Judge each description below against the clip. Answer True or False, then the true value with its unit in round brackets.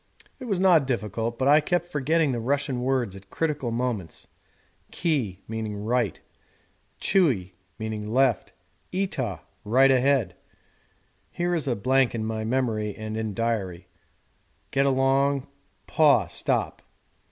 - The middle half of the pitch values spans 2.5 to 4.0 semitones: False (4.4 semitones)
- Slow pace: True (120 wpm)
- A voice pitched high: False (125 Hz)